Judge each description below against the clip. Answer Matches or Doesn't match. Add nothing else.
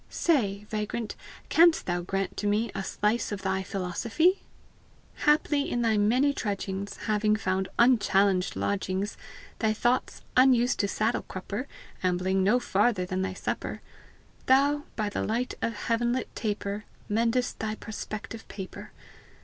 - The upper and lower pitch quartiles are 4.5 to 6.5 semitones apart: Doesn't match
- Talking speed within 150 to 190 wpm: Doesn't match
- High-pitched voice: Matches